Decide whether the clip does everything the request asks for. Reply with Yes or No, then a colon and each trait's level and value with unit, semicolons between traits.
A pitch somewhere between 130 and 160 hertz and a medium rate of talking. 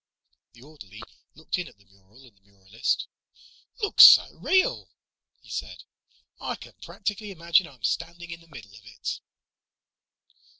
Yes: low, 135 Hz; average, 145 wpm